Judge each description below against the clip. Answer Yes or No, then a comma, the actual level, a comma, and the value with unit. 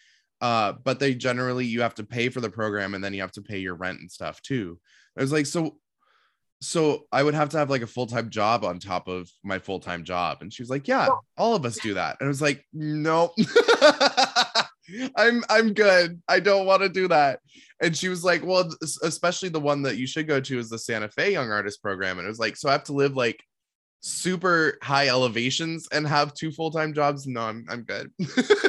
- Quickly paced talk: Yes, fast, 230 wpm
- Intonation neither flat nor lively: No, wide, 6.9 semitones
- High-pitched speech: No, medium, 140 Hz